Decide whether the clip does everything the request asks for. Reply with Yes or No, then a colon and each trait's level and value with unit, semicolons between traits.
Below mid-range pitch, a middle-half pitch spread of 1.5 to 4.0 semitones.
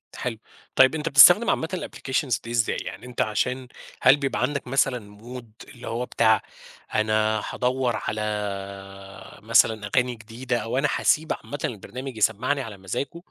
Yes: low, 125 Hz; average, 3.4 semitones